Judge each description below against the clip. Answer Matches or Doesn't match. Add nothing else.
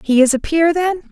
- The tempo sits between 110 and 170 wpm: Doesn't match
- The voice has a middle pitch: Doesn't match